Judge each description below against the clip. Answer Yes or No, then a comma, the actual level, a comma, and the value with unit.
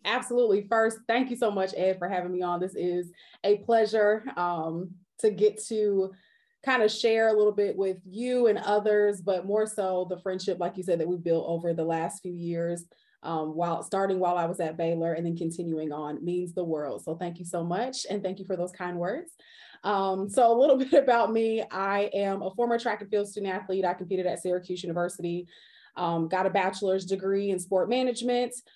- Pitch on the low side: No, high, 190 Hz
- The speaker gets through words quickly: Yes, fast, 210 wpm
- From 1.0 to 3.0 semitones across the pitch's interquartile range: No, average, 3.4 semitones